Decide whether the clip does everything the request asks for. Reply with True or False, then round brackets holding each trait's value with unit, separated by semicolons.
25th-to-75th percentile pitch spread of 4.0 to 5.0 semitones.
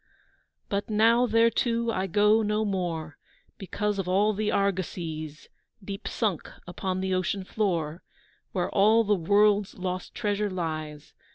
False (2.8 semitones)